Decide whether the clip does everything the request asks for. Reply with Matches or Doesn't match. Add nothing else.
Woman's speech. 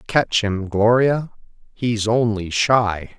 Doesn't match